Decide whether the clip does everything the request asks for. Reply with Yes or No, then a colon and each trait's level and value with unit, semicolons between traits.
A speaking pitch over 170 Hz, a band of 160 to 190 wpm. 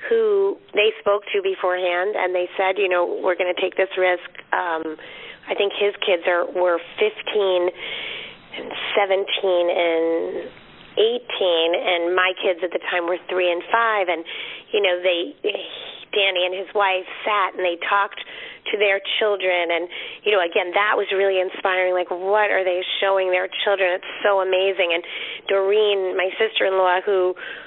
Yes: high, 190 Hz; average, 165 wpm